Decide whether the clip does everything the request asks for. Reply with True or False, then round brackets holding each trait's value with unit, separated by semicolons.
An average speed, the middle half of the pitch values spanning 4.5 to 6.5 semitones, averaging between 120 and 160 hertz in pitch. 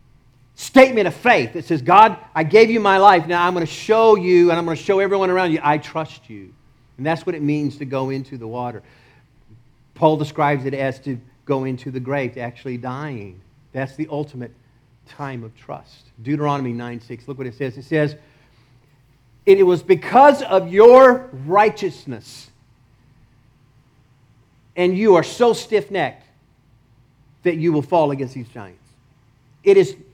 True (165 wpm; 5.1 semitones; 140 Hz)